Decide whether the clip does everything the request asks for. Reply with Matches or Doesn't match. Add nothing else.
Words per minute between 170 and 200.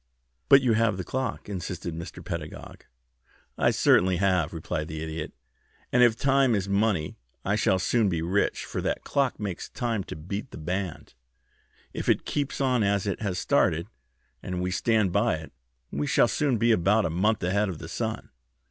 Matches